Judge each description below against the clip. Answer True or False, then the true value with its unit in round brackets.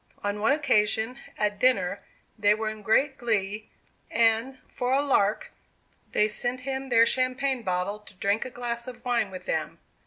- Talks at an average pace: True (165 wpm)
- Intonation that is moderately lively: True (3.4 semitones)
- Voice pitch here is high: True (225 Hz)